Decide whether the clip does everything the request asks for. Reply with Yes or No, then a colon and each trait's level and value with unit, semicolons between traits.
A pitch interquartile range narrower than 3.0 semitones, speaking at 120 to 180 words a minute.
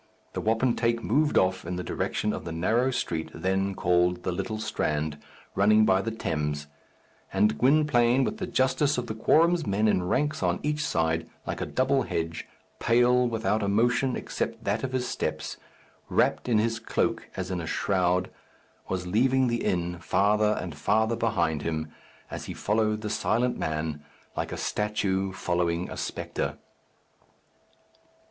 No: average, 5.1 semitones; average, 160 wpm